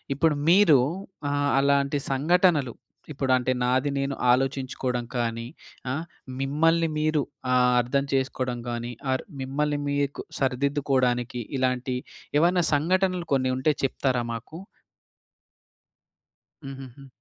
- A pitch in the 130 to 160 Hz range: Yes, low, 135 Hz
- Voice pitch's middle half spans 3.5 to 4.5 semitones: No, average, 2.7 semitones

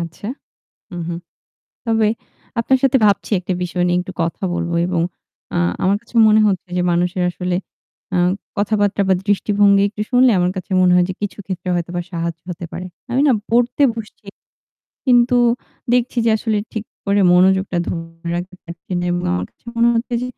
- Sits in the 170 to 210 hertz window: Yes, high, 190 Hz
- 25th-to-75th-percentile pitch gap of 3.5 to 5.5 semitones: Yes, average, 3.9 semitones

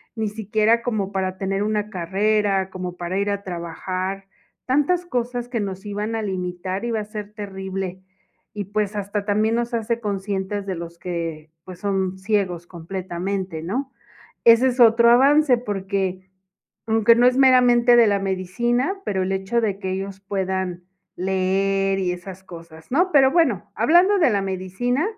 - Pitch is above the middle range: Yes, high, 200 Hz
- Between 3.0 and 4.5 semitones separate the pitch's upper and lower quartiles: Yes, average, 3.6 semitones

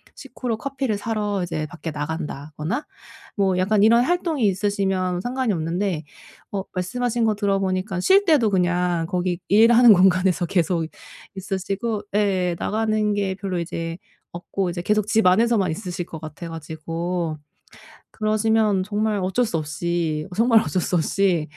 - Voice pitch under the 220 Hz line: Yes, high, 190 Hz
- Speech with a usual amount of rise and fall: Yes, average, 3.8 semitones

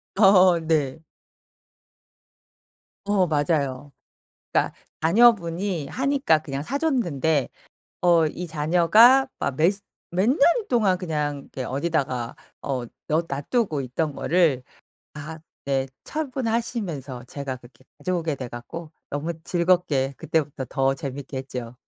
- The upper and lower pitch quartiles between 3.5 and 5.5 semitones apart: Yes, average, 5.1 semitones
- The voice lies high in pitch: No, medium, 160 Hz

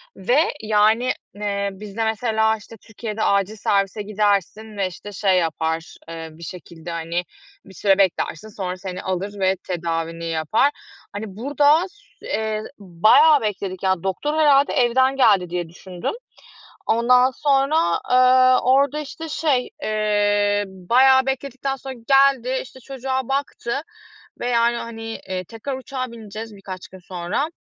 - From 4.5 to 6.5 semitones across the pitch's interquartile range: Yes, wide, 5.4 semitones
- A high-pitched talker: Yes, high, 215 Hz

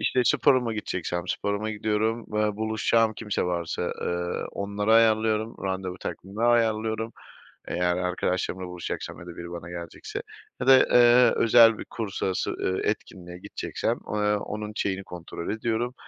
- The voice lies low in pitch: Yes, low, 105 Hz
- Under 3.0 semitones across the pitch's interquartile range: No, average, 3.6 semitones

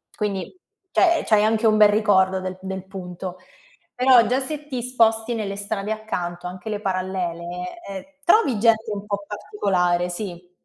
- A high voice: Yes, high, 205 Hz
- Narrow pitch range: No, average, 3.2 semitones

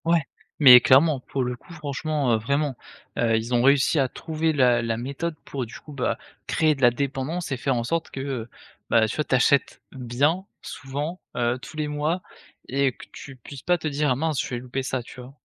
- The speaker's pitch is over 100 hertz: Yes, low, 135 Hz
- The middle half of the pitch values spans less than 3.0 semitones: No, average, 3.5 semitones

